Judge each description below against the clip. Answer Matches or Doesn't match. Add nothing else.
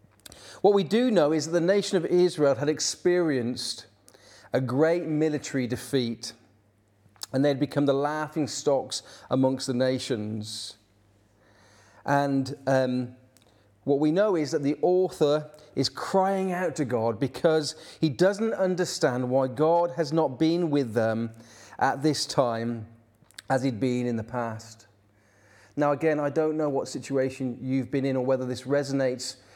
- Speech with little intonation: Doesn't match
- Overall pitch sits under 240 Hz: Matches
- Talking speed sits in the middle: Matches